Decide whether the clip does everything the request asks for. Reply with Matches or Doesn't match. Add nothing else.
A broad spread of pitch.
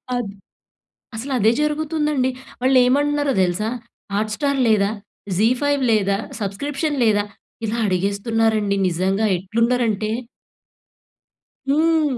Matches